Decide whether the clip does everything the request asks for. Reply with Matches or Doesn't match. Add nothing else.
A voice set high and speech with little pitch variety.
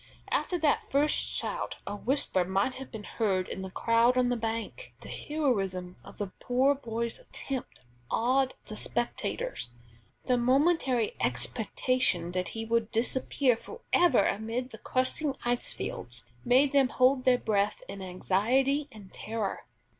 Doesn't match